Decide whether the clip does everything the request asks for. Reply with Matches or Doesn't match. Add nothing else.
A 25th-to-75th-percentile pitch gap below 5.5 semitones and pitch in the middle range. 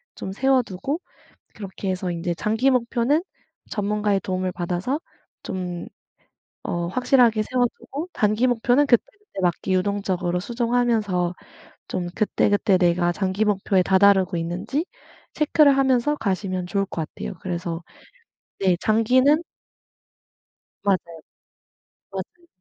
Doesn't match